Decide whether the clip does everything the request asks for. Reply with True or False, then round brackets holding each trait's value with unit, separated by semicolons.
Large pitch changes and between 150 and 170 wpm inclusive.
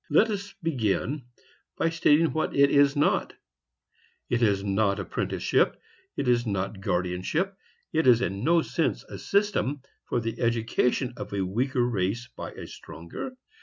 True (7.4 semitones; 165 wpm)